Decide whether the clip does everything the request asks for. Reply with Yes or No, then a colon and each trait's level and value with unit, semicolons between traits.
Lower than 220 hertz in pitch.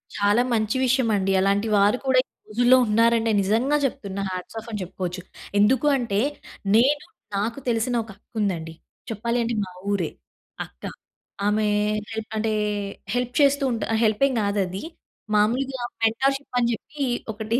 No: high, 225 Hz